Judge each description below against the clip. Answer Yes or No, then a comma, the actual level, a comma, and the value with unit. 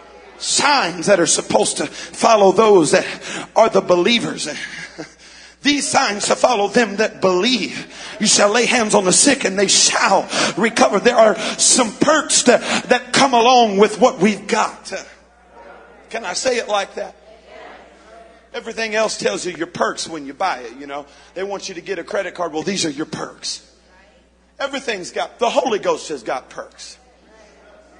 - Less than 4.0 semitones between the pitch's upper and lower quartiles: No, average, 4.3 semitones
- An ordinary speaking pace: Yes, average, 170 wpm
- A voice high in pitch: Yes, high, 215 Hz